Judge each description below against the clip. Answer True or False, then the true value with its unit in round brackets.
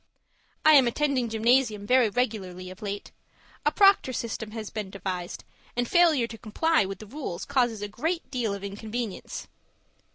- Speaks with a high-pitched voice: True (225 Hz)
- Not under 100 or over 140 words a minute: False (160 wpm)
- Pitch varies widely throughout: False (4.2 semitones)